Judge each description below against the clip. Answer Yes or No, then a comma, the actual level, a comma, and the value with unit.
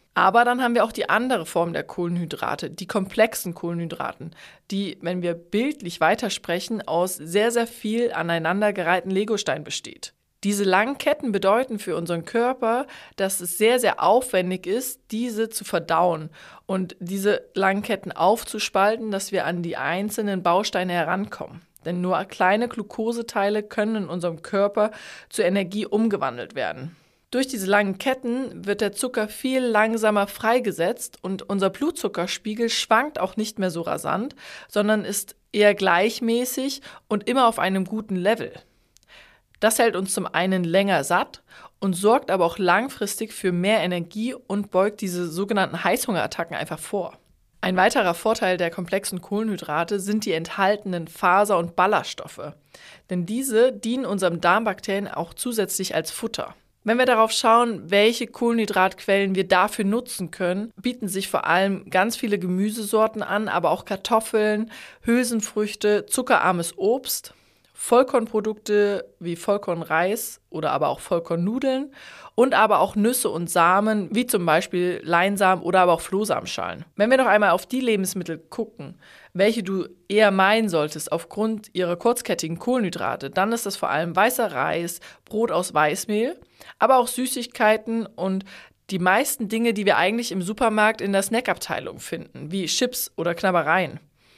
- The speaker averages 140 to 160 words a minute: Yes, average, 145 wpm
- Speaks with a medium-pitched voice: No, high, 205 Hz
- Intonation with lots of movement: No, average, 3.7 semitones